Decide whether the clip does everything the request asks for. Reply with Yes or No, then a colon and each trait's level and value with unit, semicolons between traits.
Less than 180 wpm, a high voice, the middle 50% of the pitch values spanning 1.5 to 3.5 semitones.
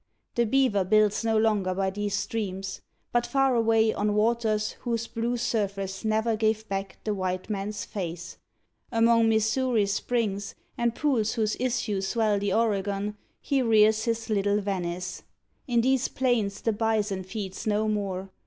Yes: average, 150 wpm; high, 215 Hz; narrow, 2.5 semitones